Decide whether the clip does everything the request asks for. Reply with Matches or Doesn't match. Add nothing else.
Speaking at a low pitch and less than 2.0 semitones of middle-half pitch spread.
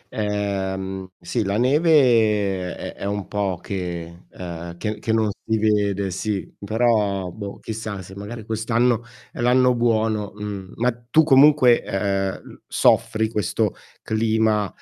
Doesn't match